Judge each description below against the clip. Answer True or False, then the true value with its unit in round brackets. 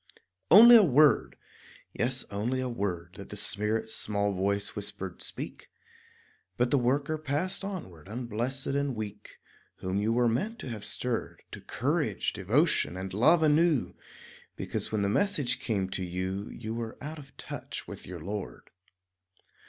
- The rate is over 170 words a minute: False (150 wpm)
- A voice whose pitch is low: True (115 Hz)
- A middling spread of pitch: False (5.9 semitones)